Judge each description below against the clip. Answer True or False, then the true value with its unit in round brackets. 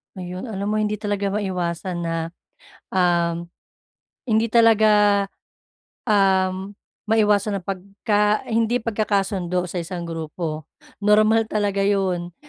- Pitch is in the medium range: False (200 Hz)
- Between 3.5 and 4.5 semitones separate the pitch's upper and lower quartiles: False (2.8 semitones)